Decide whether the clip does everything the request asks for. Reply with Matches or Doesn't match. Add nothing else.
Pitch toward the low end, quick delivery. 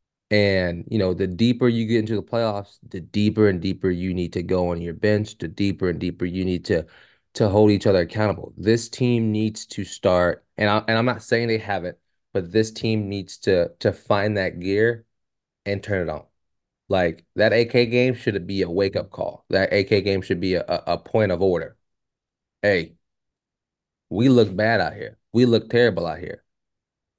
Doesn't match